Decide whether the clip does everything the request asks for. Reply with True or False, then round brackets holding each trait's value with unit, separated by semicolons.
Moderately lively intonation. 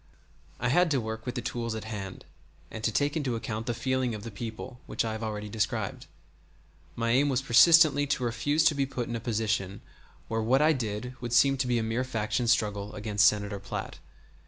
True (3.0 semitones)